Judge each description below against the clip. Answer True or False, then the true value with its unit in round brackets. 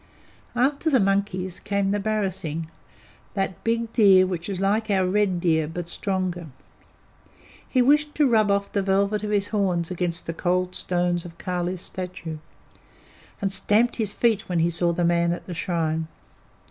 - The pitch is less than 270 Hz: True (190 Hz)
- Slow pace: False (165 wpm)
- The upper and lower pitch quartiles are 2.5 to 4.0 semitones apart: True (3.1 semitones)